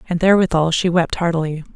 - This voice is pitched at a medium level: Yes, medium, 170 Hz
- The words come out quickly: No, average, 170 wpm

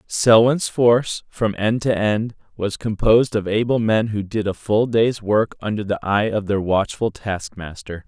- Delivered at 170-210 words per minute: Yes, average, 180 wpm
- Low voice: Yes, low, 105 Hz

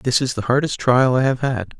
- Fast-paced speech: Yes, fast, 265 wpm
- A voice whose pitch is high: No, low, 125 Hz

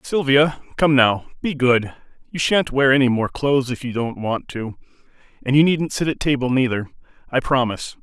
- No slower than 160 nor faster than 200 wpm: Yes, average, 185 wpm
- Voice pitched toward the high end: No, low, 130 Hz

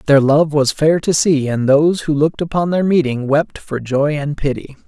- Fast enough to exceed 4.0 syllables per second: Yes, 5.0 syllables/s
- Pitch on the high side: No, medium, 150 Hz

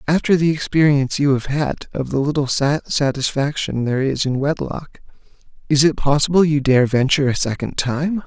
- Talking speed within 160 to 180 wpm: Yes, average, 165 wpm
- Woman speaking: No, male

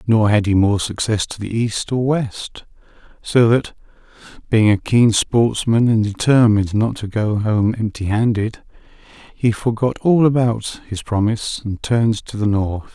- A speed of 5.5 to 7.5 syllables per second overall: No, 4.4 syllables/s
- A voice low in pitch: Yes, low, 110 Hz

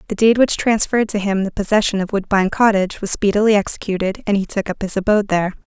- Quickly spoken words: Yes, fast, 220 wpm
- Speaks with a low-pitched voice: No, high, 200 Hz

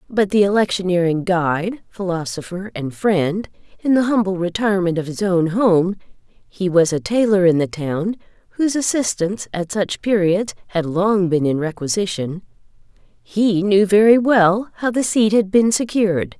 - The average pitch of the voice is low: No, high, 190 Hz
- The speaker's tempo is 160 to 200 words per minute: No, average, 145 wpm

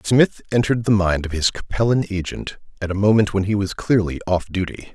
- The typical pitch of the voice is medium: No, low, 100 Hz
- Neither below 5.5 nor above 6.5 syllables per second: Yes, 5.6 syllables/s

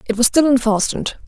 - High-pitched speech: Yes, high, 245 Hz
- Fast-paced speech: No, average, 190 wpm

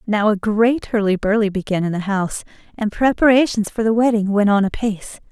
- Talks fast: No, average, 190 wpm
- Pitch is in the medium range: No, high, 210 Hz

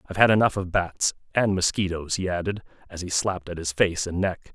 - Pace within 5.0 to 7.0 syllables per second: Yes, 5.8 syllables/s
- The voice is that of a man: Yes, male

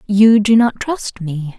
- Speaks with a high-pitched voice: Yes, high, 210 Hz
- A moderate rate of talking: Yes, average, 190 wpm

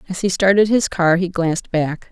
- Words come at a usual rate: No, fast, 225 wpm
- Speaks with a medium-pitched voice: Yes, medium, 180 Hz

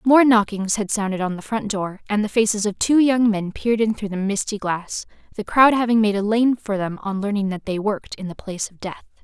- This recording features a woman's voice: Yes, female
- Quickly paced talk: Yes, fast, 255 wpm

